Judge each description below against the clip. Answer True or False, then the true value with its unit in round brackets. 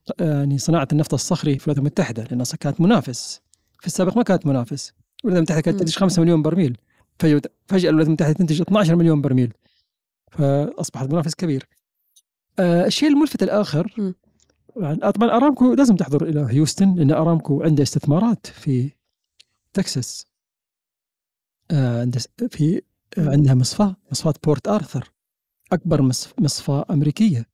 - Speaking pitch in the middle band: True (155 Hz)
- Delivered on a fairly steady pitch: False (4.8 semitones)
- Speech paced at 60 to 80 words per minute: False (125 wpm)